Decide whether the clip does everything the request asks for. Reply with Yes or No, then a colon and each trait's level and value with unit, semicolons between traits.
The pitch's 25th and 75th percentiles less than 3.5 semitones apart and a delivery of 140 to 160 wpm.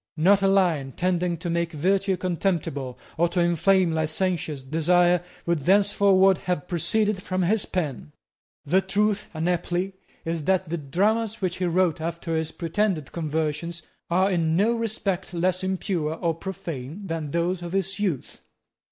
Yes: average, 2.9 semitones; average, 150 wpm